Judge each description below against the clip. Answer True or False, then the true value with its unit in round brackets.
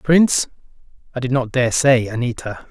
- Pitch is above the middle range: False (125 Hz)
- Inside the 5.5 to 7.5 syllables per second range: False (5.0 syllables/s)